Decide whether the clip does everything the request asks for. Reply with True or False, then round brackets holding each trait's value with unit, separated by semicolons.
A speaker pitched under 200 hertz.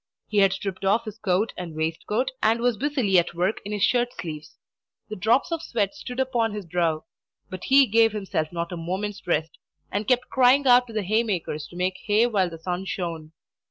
False (205 Hz)